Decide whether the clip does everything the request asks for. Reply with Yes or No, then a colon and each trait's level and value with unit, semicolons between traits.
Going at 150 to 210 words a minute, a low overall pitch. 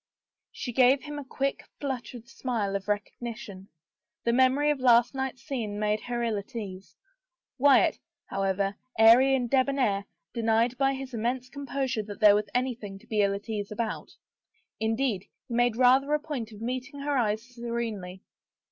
No: average, 165 wpm; high, 235 Hz